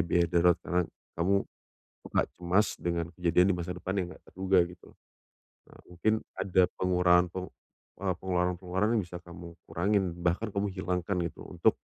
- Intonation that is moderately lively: No, narrow, 1.4 semitones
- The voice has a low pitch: Yes, very low, 90 Hz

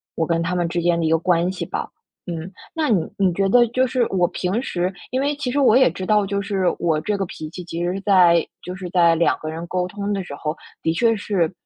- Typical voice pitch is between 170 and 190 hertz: Yes, medium, 185 Hz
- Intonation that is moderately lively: Yes, average, 3.2 semitones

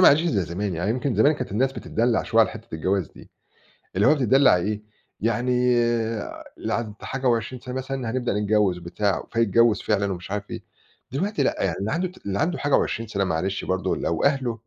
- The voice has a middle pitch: No, low, 110 Hz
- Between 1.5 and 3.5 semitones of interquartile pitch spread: No, average, 4.8 semitones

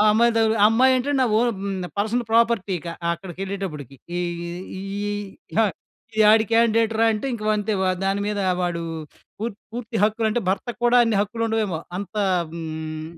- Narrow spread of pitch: No, average, 3.0 semitones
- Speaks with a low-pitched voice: No, high, 220 Hz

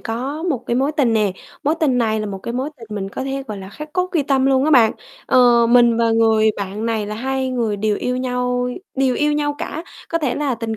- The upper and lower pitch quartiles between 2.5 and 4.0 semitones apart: Yes, average, 3.5 semitones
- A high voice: Yes, very high, 250 Hz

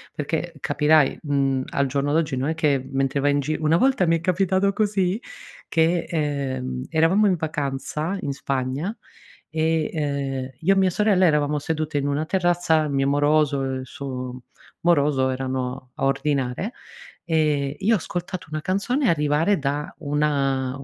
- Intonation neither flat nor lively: Yes, average, 3.5 semitones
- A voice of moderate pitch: Yes, medium, 150 Hz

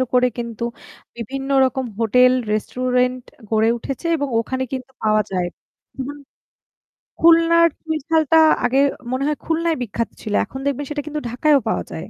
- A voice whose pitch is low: No, very high, 260 Hz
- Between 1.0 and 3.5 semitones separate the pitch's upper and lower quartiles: No, average, 4.2 semitones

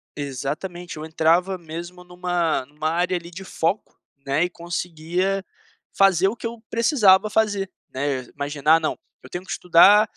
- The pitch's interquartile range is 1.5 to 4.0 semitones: Yes, average, 3.4 semitones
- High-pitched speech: No, medium, 175 Hz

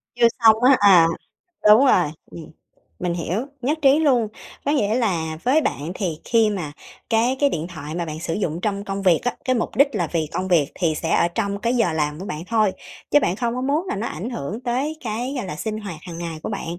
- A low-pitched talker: No, high, 200 Hz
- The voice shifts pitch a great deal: Yes, wide, 6.1 semitones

